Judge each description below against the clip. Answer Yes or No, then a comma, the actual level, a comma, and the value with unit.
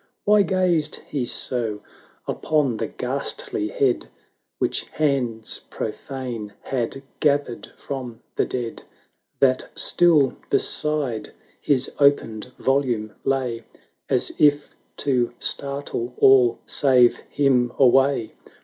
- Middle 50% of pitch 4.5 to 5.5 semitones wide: No, average, 3.1 semitones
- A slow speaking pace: Yes, slow, 105 wpm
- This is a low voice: Yes, low, 130 Hz